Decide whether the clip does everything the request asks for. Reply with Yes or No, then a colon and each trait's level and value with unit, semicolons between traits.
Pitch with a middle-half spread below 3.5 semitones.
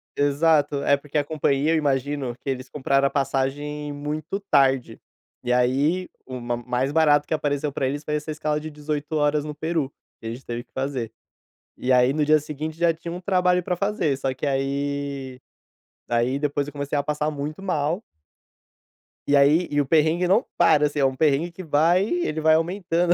Yes: narrow, 2.5 semitones